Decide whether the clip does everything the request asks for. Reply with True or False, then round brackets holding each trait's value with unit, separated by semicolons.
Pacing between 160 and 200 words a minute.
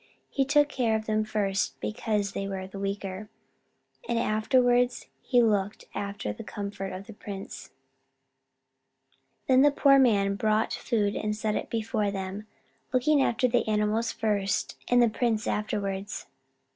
False (145 wpm)